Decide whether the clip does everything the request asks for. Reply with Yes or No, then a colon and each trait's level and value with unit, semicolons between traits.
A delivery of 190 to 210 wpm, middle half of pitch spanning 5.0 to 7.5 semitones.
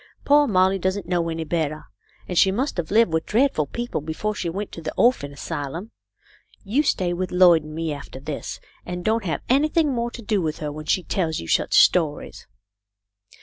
Yes: average, 200 wpm; average, 5.3 semitones